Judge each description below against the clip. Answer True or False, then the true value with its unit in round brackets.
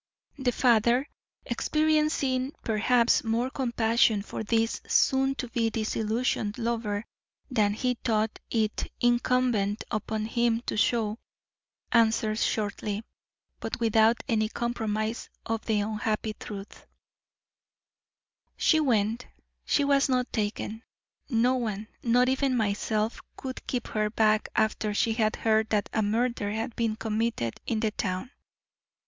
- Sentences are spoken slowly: True (125 wpm)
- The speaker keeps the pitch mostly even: True (2.2 semitones)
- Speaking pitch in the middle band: False (225 Hz)